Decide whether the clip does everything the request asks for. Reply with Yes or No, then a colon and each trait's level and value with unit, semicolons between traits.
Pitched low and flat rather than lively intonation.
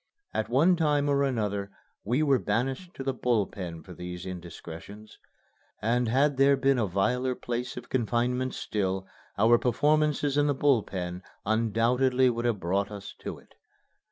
No: low, 120 Hz; average, 5.1 semitones